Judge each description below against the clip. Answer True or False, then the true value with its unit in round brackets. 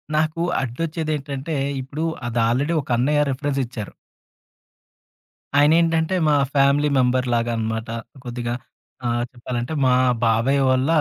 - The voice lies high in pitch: False (135 Hz)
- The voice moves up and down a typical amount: True (3.9 semitones)